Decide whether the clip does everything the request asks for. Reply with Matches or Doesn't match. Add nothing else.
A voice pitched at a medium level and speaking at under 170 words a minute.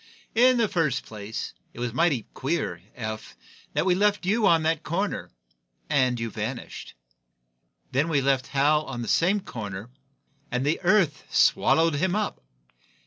Matches